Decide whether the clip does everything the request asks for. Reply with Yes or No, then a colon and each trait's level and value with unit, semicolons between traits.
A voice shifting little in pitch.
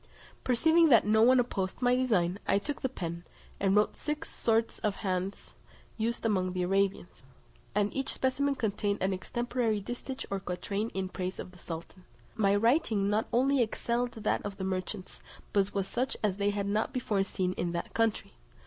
No: average, 4.1 semitones